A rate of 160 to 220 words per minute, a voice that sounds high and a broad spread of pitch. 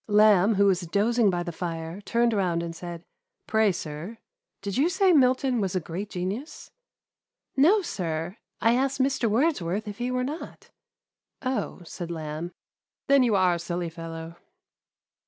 Yes: average, 175 wpm; high, 200 Hz; wide, 6.1 semitones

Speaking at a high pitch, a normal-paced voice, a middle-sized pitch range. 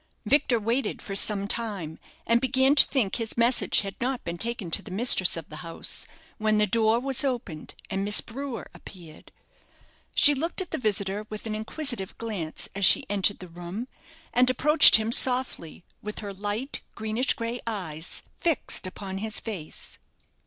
Yes: high, 215 Hz; average, 170 wpm; average, 4.3 semitones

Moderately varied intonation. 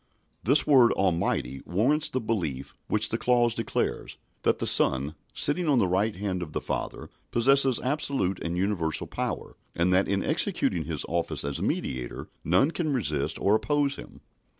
No: wide, 7.2 semitones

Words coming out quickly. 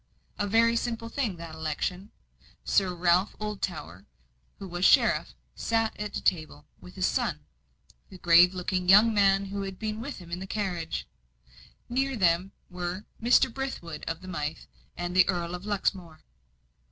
No: average, 160 wpm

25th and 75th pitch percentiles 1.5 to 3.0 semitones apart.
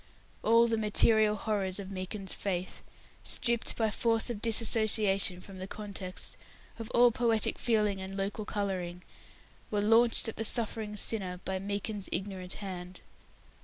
Yes: average, 2.7 semitones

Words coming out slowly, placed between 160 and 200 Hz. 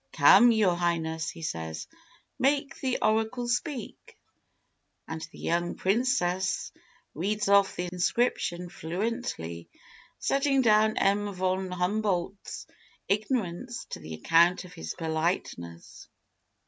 Yes: slow, 110 wpm; high, 190 Hz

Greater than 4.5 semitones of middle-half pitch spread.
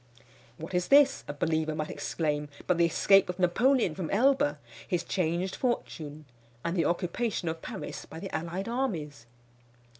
No: average, 3.7 semitones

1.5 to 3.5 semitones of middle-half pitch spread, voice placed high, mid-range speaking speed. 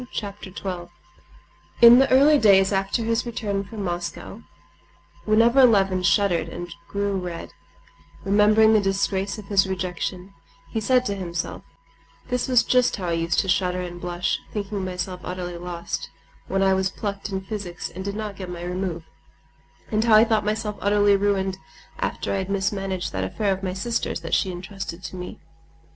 Yes: narrow, 2.6 semitones; high, 195 Hz; average, 170 wpm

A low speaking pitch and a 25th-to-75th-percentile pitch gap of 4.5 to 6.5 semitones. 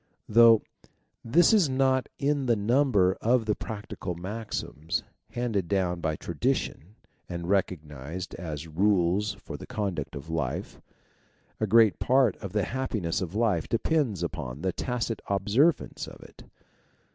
Yes: low, 100 Hz; wide, 5.4 semitones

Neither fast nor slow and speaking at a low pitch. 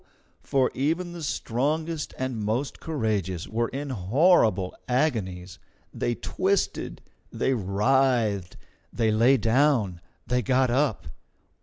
No: slow, 110 wpm; low, 125 Hz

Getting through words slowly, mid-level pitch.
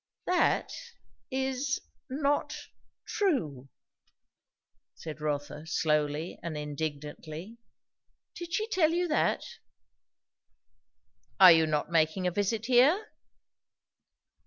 Yes: slow, 85 wpm; medium, 180 Hz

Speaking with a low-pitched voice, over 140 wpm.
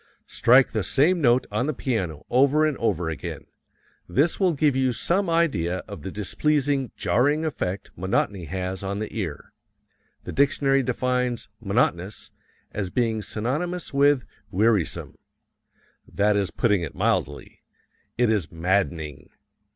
No: low, 115 Hz; slow, 135 wpm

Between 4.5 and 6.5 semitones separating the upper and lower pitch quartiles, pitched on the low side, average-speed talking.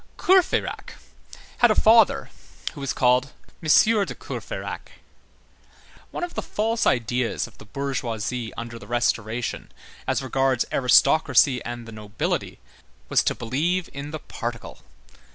No: average, 5.0 semitones; low, 130 Hz; slow, 130 wpm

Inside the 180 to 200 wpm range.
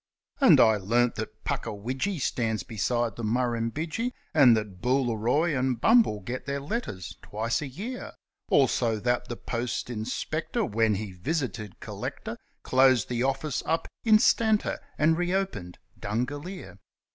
No: slow, 135 wpm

